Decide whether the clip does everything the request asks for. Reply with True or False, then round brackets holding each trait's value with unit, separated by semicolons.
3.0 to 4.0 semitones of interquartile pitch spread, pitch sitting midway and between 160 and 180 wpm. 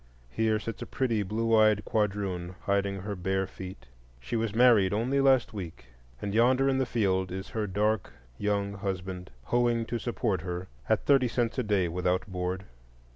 False (3.4 semitones; 105 Hz; 175 wpm)